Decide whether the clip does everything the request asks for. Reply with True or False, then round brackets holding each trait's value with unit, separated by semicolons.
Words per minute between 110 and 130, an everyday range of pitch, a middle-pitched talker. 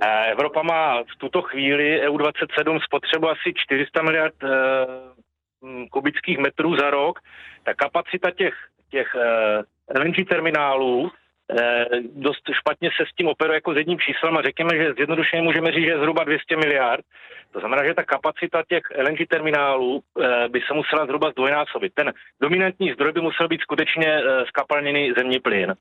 False (165 wpm; 3.6 semitones; 150 Hz)